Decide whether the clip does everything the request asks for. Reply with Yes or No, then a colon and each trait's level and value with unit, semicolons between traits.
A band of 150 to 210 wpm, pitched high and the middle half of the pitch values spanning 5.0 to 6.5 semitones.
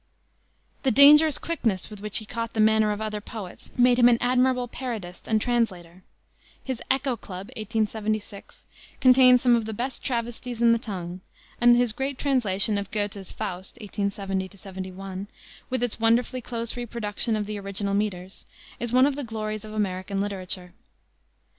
No: average, 160 wpm; high, 220 Hz; average, 3.5 semitones